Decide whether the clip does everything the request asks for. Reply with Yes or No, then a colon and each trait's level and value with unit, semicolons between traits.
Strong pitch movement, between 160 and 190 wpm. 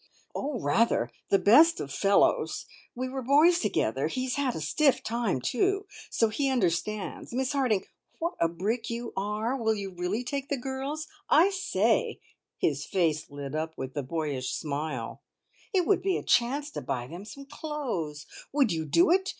Yes: wide, 8.9 semitones; average, 175 wpm